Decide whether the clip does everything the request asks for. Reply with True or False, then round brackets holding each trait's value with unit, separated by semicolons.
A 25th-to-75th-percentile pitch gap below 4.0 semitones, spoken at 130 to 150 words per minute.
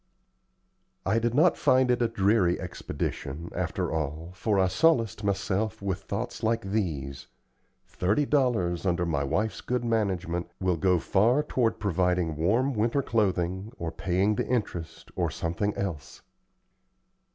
False (4.7 semitones; 140 wpm)